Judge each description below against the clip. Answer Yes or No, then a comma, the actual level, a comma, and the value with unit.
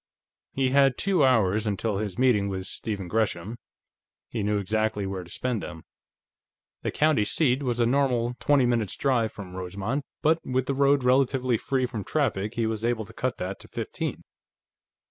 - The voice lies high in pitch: No, low, 115 Hz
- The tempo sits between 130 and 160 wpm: No, average, 175 wpm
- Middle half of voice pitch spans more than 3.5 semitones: Yes, average, 4.3 semitones